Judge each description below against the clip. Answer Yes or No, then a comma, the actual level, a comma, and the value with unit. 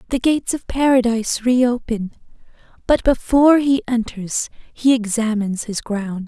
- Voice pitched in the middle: No, high, 235 Hz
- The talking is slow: Yes, slow, 125 wpm